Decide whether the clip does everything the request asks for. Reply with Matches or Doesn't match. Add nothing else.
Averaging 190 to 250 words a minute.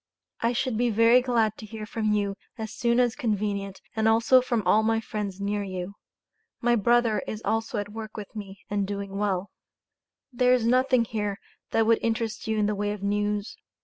Matches